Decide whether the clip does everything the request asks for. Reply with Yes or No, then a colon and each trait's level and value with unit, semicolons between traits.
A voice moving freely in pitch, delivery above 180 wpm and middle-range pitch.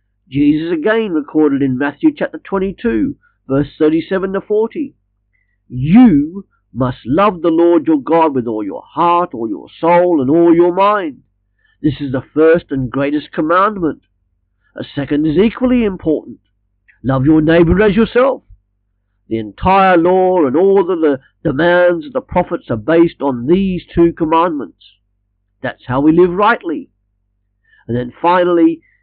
No: wide, 6.9 semitones; average, 145 wpm; medium, 160 Hz